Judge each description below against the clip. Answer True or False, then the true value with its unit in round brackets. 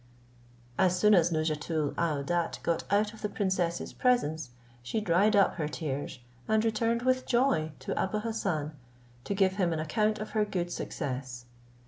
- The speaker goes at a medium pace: True (160 wpm)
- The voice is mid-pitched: True (180 Hz)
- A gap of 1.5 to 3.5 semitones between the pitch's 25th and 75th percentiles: False (5.4 semitones)